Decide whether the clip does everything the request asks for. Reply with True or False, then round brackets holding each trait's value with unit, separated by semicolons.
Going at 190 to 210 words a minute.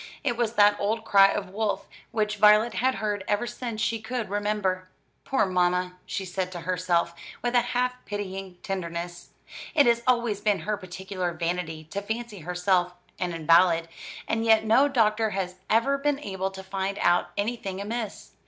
False (170 wpm)